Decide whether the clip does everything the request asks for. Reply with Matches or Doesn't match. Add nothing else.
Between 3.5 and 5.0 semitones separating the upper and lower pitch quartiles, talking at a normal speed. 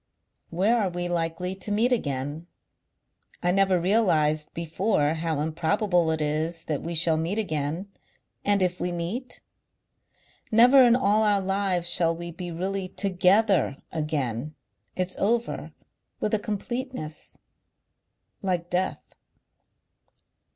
Doesn't match